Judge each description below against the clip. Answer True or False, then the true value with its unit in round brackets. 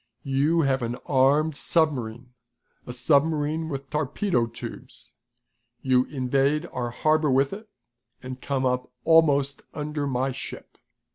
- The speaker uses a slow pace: True (125 wpm)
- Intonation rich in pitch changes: False (3.1 semitones)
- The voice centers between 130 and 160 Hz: True (140 Hz)